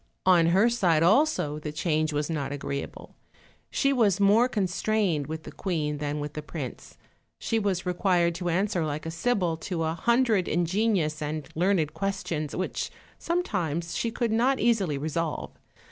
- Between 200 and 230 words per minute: No, average, 160 wpm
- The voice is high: No, medium, 175 Hz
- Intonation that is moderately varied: Yes, average, 4.9 semitones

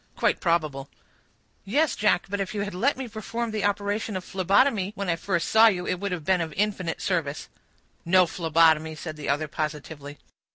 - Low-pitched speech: No, medium, 185 Hz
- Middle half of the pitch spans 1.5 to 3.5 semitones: No, average, 4.2 semitones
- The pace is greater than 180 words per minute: Yes, average, 190 wpm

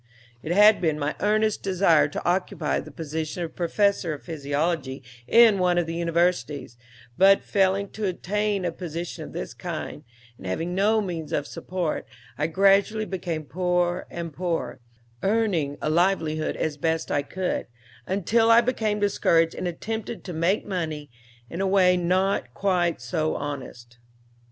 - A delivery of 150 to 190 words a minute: Yes, average, 155 wpm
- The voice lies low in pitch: No, medium, 175 Hz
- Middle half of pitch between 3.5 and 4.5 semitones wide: Yes, average, 3.8 semitones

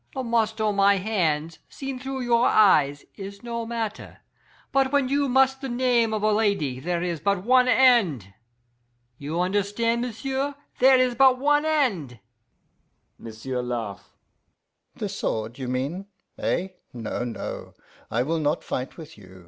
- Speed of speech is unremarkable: Yes, average, 150 wpm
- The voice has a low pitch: No, high, 205 Hz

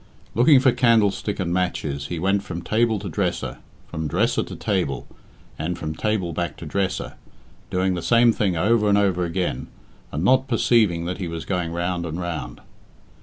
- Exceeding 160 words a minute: Yes, average, 175 wpm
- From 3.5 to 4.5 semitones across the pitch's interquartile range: Yes, average, 3.9 semitones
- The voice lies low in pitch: Yes, very low, 90 Hz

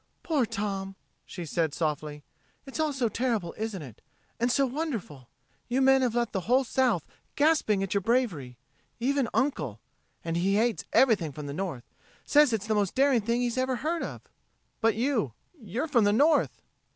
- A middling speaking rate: Yes, average, 175 wpm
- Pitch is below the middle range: No, high, 225 Hz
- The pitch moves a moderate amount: No, wide, 6.7 semitones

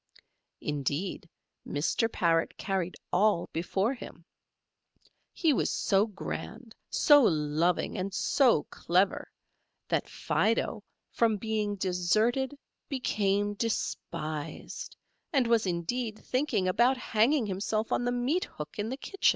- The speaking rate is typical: No, slow, 115 wpm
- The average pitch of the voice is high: Yes, high, 210 Hz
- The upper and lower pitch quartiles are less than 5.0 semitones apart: No, average, 5.3 semitones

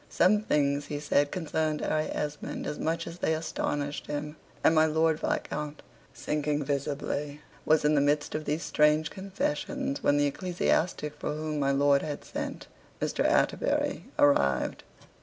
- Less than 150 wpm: No, average, 155 wpm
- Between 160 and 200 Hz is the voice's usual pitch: No, medium, 150 Hz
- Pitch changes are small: Yes, narrow, 1.5 semitones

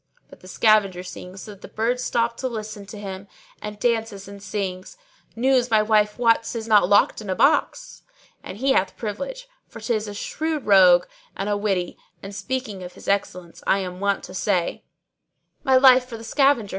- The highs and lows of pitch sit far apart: No, average, 3.6 semitones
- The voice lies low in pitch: No, high, 210 Hz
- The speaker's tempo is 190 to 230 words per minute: Yes, average, 195 wpm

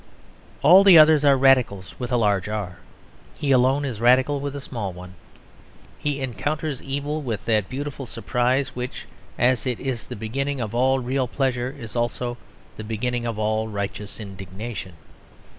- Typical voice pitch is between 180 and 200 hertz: No, low, 125 Hz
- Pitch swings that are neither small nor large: Yes, average, 4.0 semitones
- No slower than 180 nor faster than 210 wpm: No, average, 160 wpm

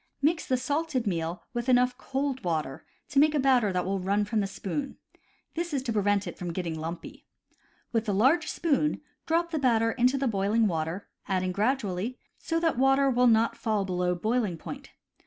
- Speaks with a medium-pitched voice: No, high, 230 Hz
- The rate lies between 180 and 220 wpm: Yes, average, 190 wpm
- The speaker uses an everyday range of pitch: No, wide, 6.0 semitones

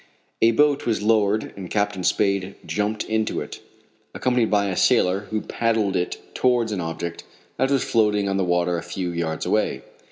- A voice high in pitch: No, low, 105 Hz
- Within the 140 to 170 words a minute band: No, average, 180 wpm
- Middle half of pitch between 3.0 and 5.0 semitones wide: Yes, average, 3.4 semitones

